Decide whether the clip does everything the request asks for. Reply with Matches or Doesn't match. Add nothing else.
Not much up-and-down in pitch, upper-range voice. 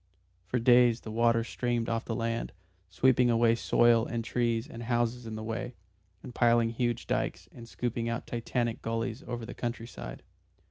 Doesn't match